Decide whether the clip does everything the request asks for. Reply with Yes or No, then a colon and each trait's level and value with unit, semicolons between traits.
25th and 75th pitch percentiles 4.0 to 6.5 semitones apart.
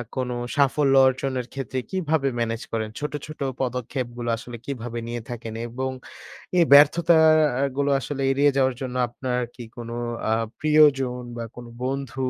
No: average, 2.8 semitones